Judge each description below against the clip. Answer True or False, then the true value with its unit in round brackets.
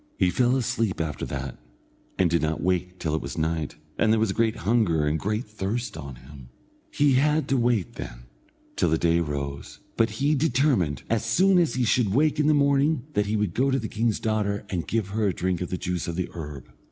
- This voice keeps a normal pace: False (225 wpm)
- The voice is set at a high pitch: False (105 Hz)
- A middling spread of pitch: False (6.6 semitones)